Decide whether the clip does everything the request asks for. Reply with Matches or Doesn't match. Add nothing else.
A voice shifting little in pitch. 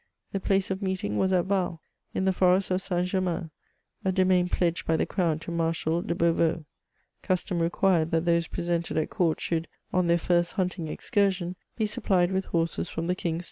Matches